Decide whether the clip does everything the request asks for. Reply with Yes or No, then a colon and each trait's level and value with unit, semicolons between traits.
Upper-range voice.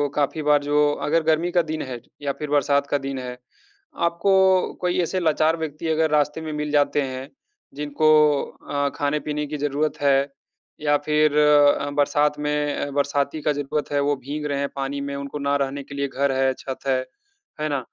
No: medium, 145 Hz